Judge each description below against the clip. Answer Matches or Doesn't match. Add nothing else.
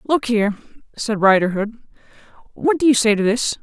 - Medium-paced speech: Matches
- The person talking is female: Matches